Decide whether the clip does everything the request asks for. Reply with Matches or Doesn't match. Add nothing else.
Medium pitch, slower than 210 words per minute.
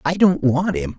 Doesn't match